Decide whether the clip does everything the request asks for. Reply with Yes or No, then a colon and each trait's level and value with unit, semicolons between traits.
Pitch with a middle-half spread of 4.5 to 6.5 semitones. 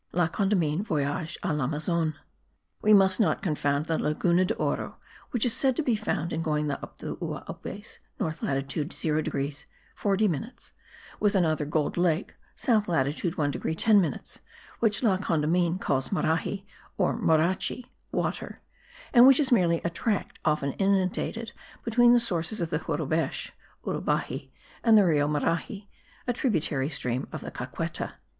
Yes: wide, 5.4 semitones